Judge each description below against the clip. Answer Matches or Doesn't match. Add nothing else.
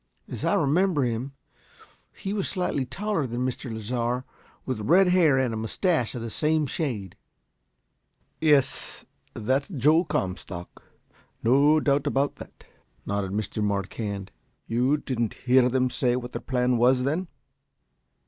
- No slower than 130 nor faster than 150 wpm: Matches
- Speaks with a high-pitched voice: Doesn't match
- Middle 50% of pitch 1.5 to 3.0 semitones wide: Doesn't match